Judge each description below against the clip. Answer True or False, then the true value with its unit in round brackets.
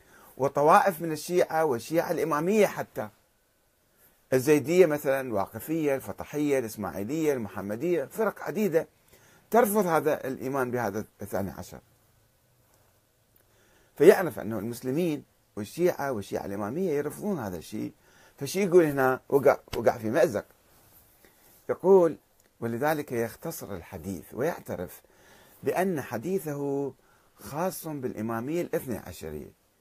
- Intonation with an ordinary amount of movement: False (7.5 semitones)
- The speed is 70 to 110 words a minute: True (95 wpm)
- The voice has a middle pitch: False (130 Hz)